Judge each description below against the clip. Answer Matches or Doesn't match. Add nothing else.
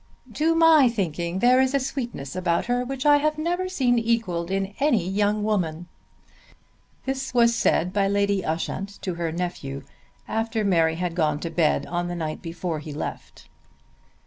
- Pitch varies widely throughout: Matches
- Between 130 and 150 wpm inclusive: Doesn't match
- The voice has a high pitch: Matches